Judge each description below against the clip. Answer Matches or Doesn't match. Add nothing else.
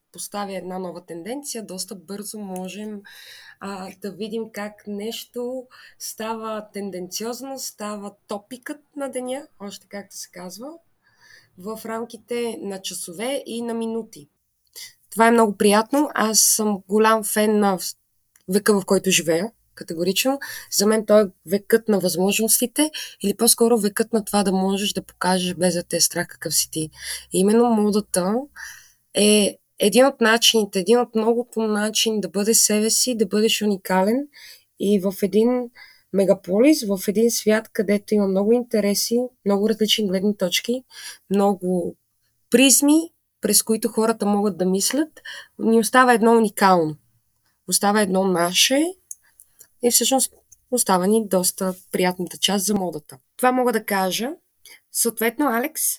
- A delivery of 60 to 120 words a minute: Doesn't match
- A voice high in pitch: Matches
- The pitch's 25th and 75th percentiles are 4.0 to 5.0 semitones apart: Doesn't match